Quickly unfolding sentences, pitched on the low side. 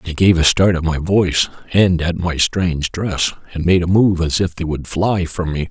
Yes: fast, 240 wpm; very low, 85 Hz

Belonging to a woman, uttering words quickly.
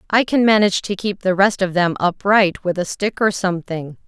Yes: female; fast, 220 wpm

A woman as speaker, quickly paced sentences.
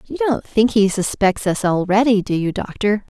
No: female; average, 190 wpm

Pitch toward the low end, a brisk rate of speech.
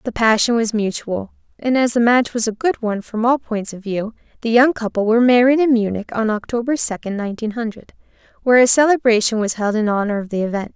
No: high, 225 Hz; fast, 220 wpm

